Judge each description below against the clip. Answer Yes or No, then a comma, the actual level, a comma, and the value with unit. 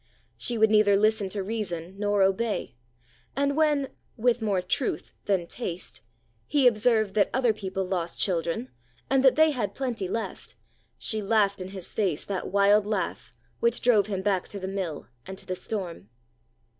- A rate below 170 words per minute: Yes, average, 160 wpm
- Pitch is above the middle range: Yes, high, 205 Hz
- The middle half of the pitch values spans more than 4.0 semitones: No, average, 3.4 semitones